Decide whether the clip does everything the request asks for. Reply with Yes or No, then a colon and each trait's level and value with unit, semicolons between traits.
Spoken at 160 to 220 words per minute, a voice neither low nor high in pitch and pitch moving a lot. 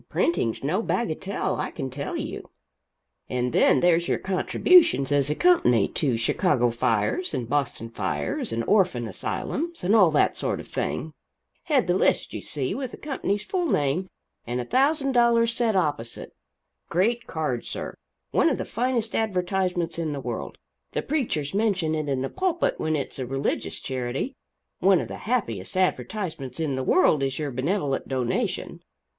Yes: average, 165 wpm; medium, 165 Hz; wide, 8.5 semitones